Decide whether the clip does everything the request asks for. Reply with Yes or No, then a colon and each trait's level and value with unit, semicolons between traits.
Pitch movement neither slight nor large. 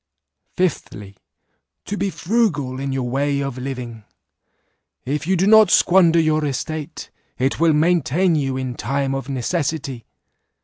Yes: average, 4.2 semitones